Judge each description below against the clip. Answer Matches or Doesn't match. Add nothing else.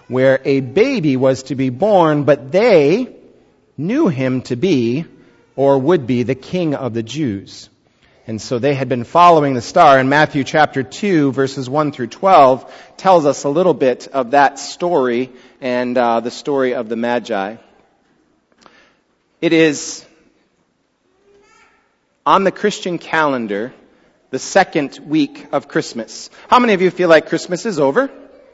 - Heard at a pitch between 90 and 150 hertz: Matches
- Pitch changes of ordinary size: Doesn't match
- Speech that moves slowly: Doesn't match